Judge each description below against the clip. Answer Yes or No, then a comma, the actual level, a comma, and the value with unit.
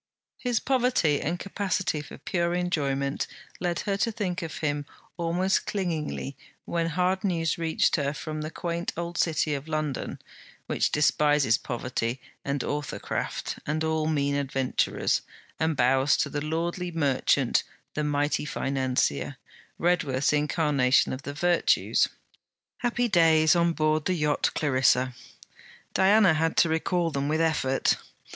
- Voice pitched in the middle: Yes, medium, 155 Hz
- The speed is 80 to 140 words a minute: Yes, slow, 135 wpm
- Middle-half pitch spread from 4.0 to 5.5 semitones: No, average, 3.3 semitones